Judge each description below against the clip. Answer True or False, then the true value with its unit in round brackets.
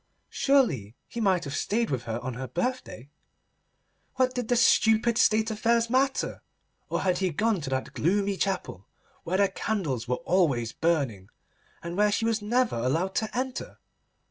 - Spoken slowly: False (165 wpm)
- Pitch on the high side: True (195 Hz)